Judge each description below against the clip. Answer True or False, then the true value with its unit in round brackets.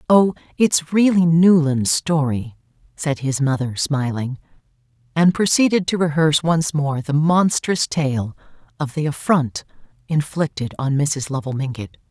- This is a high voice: False (150 Hz)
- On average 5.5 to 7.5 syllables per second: False (4.3 syllables/s)